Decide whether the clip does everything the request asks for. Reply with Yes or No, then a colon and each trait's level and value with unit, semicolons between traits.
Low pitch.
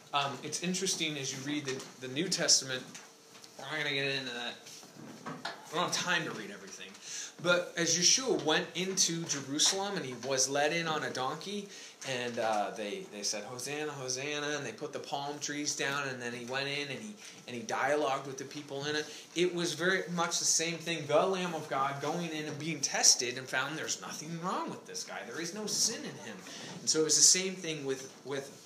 No: medium, 150 Hz